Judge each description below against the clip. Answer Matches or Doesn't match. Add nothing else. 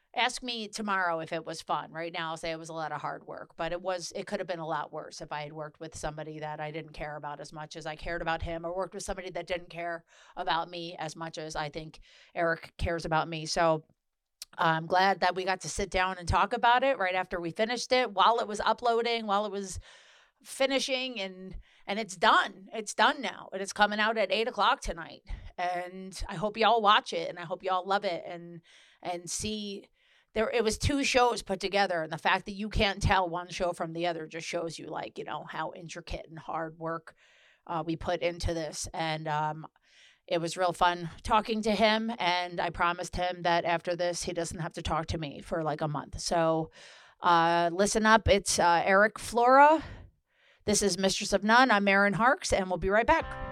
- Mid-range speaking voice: Matches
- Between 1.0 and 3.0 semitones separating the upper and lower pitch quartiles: Doesn't match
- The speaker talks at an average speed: Doesn't match